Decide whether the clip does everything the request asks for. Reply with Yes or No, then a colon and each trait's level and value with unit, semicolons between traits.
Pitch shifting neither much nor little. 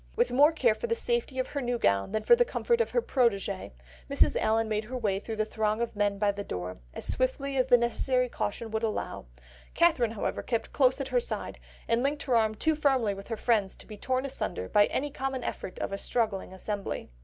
Yes: average, 4.4 semitones